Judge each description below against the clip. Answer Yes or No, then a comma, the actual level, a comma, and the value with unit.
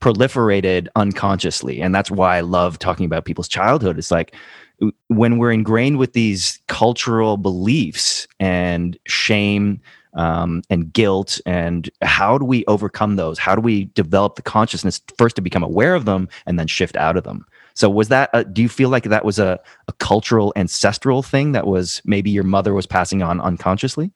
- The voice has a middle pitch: No, low, 100 Hz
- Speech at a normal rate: Yes, average, 180 wpm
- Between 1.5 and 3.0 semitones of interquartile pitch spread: No, average, 3.7 semitones